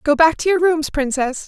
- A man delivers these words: No, female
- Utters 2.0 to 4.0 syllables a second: No, 5.1 syllables/s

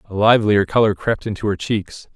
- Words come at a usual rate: Yes, average, 195 wpm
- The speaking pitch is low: Yes, low, 105 Hz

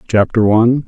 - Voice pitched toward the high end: No, low, 115 Hz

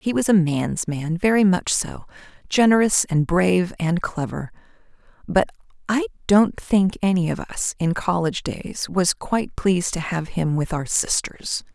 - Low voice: No, medium, 180 Hz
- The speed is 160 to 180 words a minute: Yes, average, 165 wpm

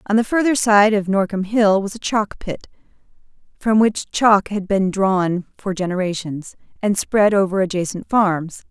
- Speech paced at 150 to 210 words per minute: Yes, average, 165 wpm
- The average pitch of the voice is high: Yes, high, 200 Hz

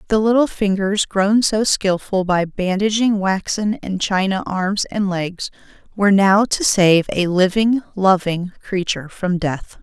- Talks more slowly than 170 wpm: Yes, average, 145 wpm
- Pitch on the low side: No, high, 195 Hz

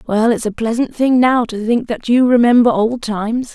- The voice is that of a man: No, female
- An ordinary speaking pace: No, fast, 220 wpm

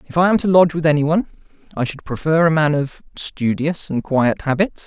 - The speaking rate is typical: No, fast, 210 wpm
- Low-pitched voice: No, medium, 155 Hz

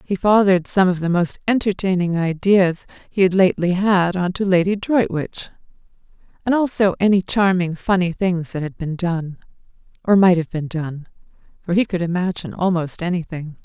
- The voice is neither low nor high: Yes, medium, 180 Hz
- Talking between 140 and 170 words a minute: Yes, average, 160 wpm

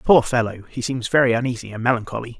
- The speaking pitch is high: No, low, 120 Hz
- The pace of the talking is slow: No, average, 200 wpm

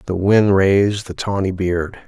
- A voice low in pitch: Yes, very low, 95 Hz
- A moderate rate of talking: Yes, average, 175 wpm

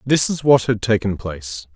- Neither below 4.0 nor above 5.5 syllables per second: Yes, 5.1 syllables/s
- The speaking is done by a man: Yes, male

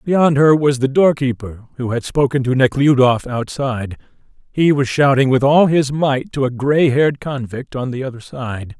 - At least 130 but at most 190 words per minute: Yes, average, 175 wpm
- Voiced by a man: Yes, male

